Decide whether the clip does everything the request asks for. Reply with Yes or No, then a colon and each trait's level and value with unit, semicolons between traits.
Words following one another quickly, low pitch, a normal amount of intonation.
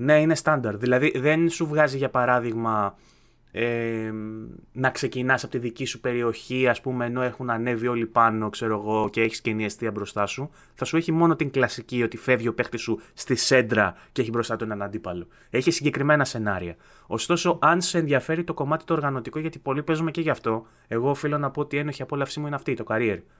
Yes: fast, 210 wpm; low, 125 Hz; average, 4.6 semitones